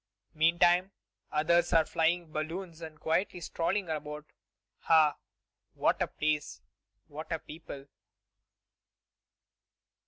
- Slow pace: Yes, slow, 95 wpm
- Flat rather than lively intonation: Yes, narrow, 2.0 semitones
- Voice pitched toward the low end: No, medium, 160 Hz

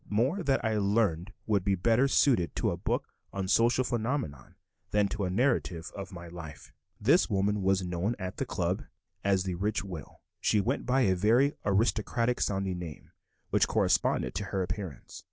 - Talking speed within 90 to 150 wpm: No, average, 175 wpm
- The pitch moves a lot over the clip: No, average, 4.1 semitones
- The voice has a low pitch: Yes, low, 100 Hz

